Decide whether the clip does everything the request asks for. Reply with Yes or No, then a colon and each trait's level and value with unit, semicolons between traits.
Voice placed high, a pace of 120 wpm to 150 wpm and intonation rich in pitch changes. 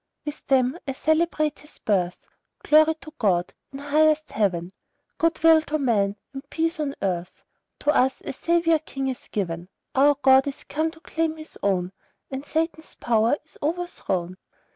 No: very high, 280 Hz; average, 165 wpm; wide, 6.8 semitones